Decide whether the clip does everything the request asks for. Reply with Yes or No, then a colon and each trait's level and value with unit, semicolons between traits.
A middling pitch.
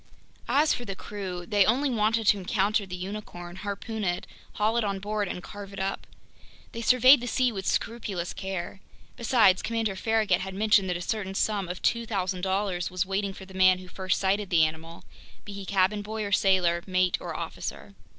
No: high, 195 Hz